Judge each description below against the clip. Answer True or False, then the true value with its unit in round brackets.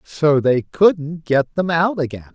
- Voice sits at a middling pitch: True (155 Hz)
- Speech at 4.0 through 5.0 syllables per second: False (3.7 syllables/s)